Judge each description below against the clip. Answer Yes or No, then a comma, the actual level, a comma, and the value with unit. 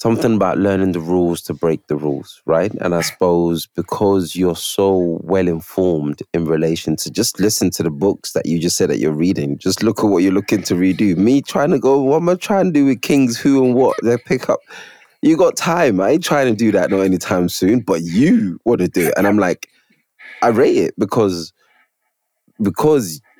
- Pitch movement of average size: No, wide, 5.7 semitones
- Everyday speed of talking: No, fast, 220 wpm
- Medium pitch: No, very low, 95 Hz